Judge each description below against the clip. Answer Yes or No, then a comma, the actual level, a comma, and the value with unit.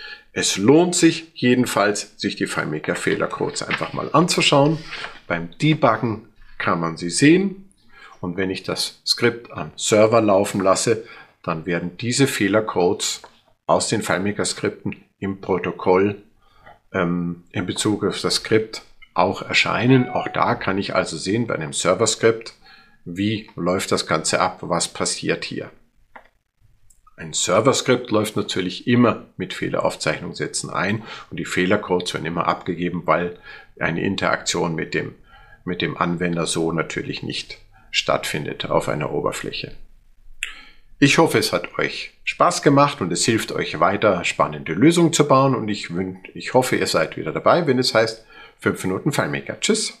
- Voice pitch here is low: Yes, low, 105 Hz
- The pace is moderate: Yes, average, 145 wpm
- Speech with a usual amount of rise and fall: No, wide, 7.6 semitones